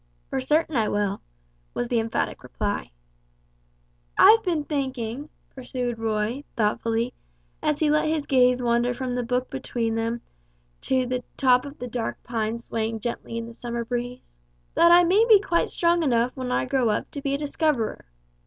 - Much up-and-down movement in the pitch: No, average, 3.5 semitones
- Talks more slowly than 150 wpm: No, average, 170 wpm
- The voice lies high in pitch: Yes, very high, 250 Hz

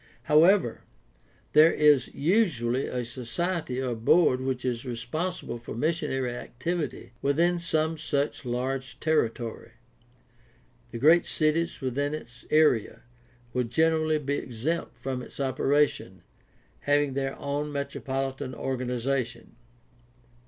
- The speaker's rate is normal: No, slow, 110 wpm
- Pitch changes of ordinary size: Yes, average, 3.9 semitones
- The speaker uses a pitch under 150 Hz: Yes, low, 135 Hz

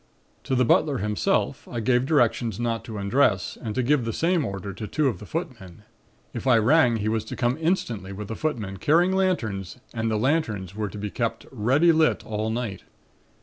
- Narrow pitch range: No, average, 5.0 semitones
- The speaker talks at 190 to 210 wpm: Yes, average, 200 wpm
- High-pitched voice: No, low, 115 Hz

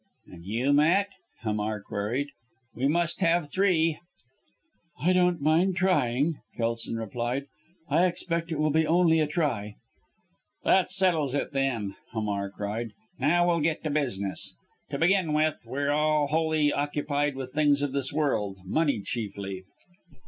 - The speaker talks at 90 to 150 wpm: Yes, average, 140 wpm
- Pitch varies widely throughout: Yes, wide, 5.8 semitones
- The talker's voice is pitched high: No, medium, 145 Hz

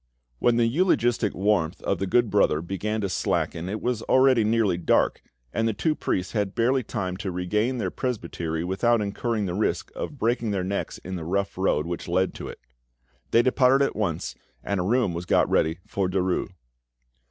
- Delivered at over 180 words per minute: Yes, average, 190 wpm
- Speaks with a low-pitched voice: Yes, low, 100 Hz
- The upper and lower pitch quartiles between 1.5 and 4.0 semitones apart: No, average, 4.4 semitones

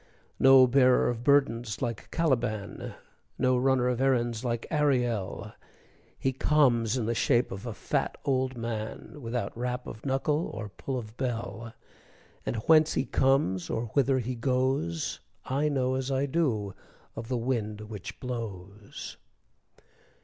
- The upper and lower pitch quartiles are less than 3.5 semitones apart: Yes, average, 2.9 semitones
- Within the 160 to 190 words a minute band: No, average, 140 wpm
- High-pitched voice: No, low, 125 Hz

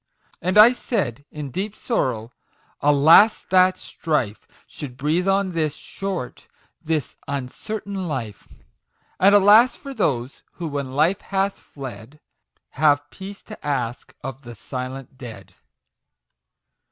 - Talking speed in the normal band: No, slow, 125 wpm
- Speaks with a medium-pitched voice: Yes, medium, 150 Hz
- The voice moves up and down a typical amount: No, wide, 6.8 semitones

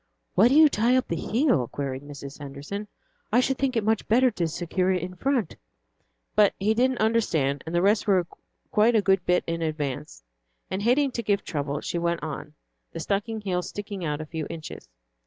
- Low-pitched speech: No, high, 190 Hz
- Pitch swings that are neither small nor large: No, wide, 6.3 semitones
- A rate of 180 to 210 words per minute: Yes, average, 200 wpm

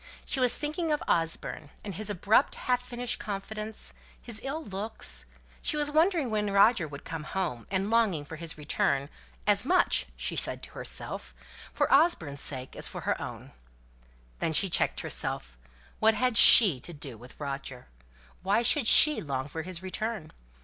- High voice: Yes, high, 200 Hz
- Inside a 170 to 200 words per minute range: Yes, average, 175 wpm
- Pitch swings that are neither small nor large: No, wide, 7.8 semitones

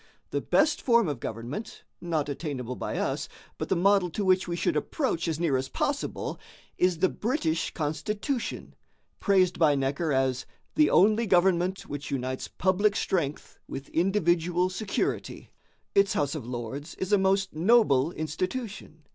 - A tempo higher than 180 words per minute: No, average, 150 wpm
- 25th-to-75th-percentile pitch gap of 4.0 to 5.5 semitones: Yes, average, 5.1 semitones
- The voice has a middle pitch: Yes, medium, 175 Hz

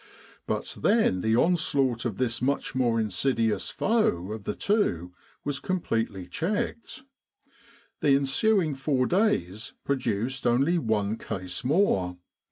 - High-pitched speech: No, low, 125 Hz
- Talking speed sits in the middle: No, slow, 120 wpm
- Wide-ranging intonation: Yes, wide, 6.8 semitones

